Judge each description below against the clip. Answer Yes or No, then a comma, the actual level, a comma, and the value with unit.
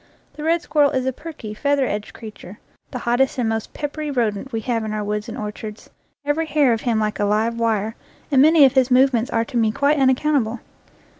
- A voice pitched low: No, high, 245 Hz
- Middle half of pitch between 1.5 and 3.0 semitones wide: No, average, 4.6 semitones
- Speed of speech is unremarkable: No, fast, 225 wpm